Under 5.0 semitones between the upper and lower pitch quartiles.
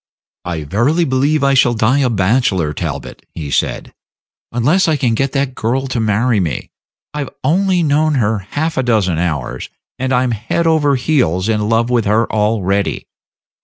No: wide, 5.4 semitones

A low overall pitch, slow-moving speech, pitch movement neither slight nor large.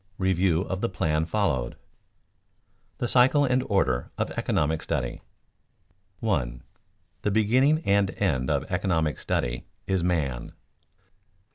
No: very low, 90 Hz; slow, 120 wpm; wide, 6.3 semitones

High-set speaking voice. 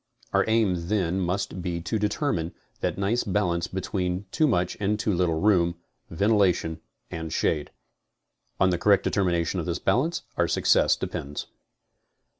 No: very low, 90 Hz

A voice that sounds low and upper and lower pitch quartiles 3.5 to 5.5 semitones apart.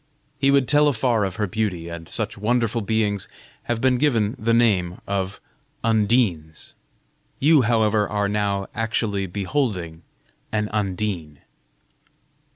No: low, 105 Hz; average, 3.1 semitones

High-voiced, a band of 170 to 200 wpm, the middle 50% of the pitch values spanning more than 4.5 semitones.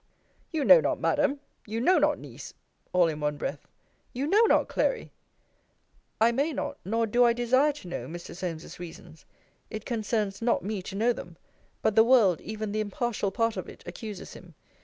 Yes: high, 220 Hz; average, 185 wpm; average, 4.9 semitones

